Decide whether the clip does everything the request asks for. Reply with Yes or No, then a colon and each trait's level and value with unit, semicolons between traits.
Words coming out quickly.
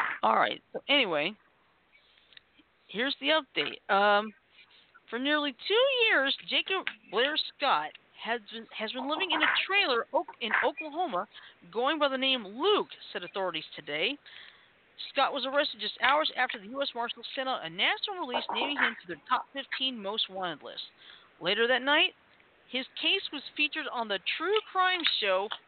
No: average, 155 wpm